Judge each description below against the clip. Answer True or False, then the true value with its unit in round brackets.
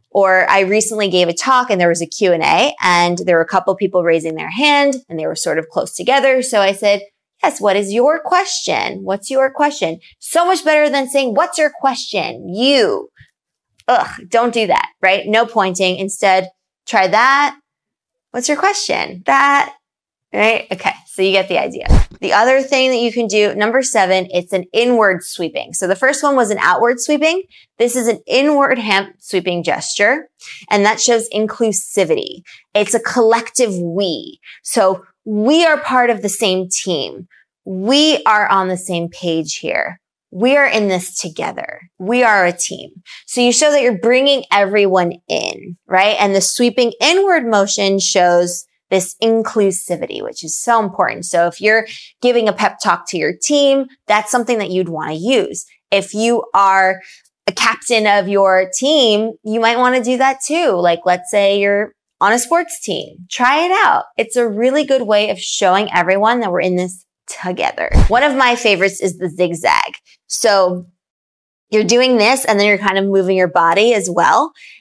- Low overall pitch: False (210 Hz)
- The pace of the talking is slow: False (185 wpm)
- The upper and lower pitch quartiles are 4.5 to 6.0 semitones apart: True (5.1 semitones)